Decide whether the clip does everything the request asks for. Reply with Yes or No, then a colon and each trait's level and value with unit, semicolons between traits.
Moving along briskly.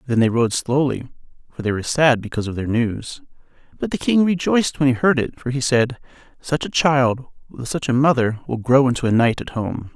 Yes: fast, 225 wpm